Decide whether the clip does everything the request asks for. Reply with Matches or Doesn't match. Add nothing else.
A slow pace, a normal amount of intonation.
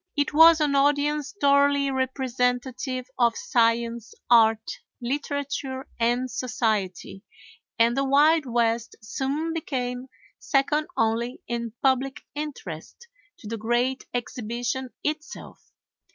Matches